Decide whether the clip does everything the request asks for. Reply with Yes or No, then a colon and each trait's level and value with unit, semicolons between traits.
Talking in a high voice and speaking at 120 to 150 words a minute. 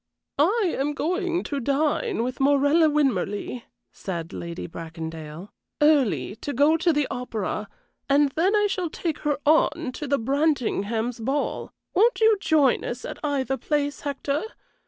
Yes: very high, 285 Hz; average, 145 wpm